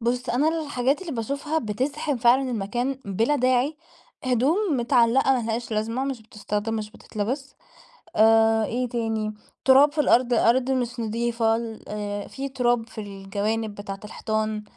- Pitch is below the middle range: No, high, 235 Hz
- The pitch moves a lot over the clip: No, average, 3.2 semitones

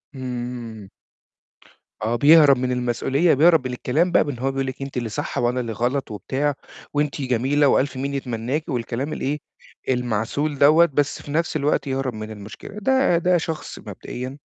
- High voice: No, low, 135 Hz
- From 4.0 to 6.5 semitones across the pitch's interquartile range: No, average, 3.2 semitones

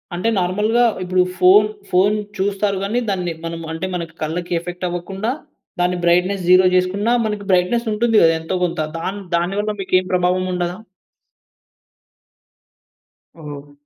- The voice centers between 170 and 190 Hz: Yes, medium, 185 Hz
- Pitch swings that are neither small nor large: No, narrow, 2.3 semitones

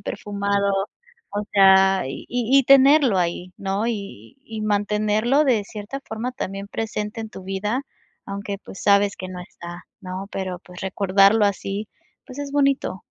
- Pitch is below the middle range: No, high, 205 Hz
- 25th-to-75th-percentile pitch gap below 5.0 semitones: Yes, narrow, 2.6 semitones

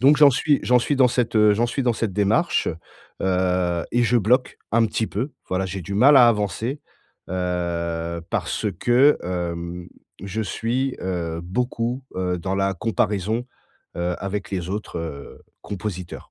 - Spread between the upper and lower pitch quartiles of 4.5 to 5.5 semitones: Yes, average, 5.1 semitones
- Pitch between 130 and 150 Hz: No, low, 100 Hz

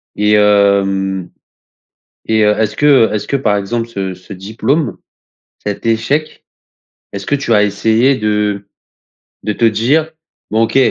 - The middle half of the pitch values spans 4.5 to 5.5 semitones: No, average, 2.7 semitones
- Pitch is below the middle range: Yes, low, 105 Hz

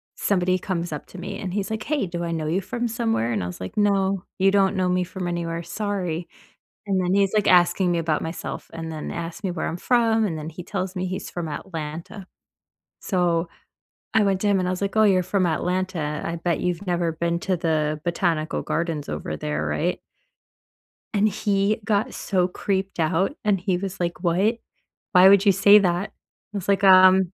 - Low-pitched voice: No, medium, 180 Hz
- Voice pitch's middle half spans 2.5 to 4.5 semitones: Yes, average, 2.8 semitones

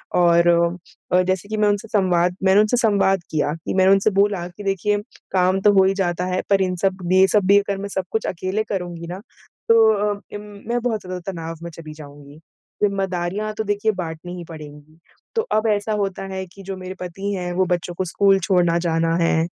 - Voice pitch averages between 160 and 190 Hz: Yes, medium, 185 Hz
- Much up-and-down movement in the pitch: No, average, 2.7 semitones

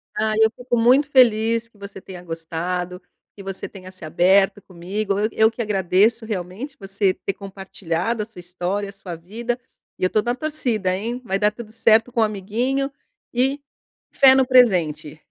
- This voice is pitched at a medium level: No, high, 210 Hz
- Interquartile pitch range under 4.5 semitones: Yes, average, 4.1 semitones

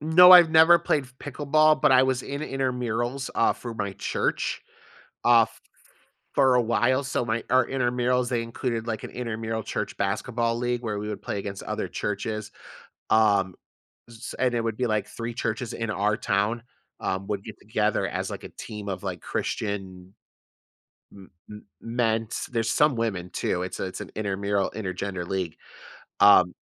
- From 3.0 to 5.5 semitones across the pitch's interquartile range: Yes, average, 3.6 semitones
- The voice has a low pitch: Yes, low, 115 Hz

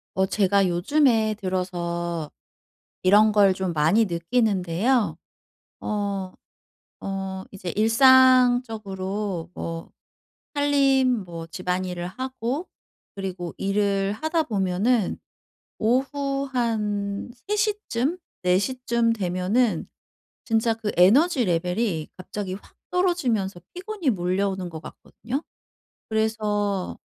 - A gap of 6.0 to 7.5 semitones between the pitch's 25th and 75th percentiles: No, average, 5.2 semitones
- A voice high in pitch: Yes, high, 205 Hz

